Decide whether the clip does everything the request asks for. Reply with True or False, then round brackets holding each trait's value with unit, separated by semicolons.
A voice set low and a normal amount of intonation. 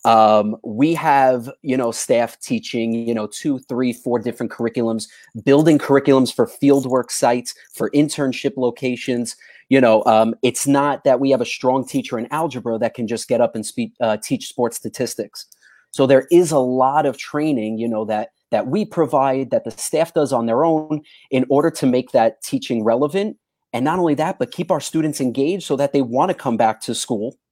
True (130 Hz; 4.1 semitones)